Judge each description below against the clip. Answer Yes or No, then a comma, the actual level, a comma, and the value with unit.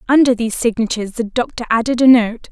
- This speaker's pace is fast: No, average, 190 wpm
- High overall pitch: Yes, high, 235 Hz